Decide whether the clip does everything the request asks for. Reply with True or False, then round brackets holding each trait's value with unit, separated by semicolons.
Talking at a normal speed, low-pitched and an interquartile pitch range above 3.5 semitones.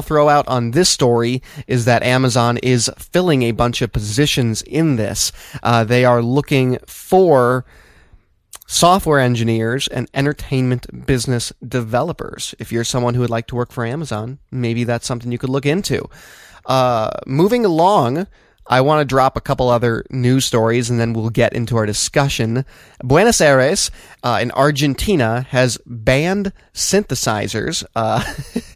False (150 wpm; 125 Hz; 2.8 semitones)